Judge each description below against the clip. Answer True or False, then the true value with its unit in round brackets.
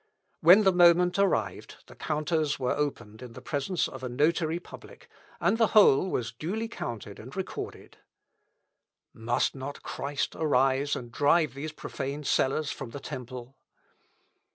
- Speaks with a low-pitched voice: False (145 Hz)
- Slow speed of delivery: False (145 wpm)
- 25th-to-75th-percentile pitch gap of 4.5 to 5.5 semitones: True (4.9 semitones)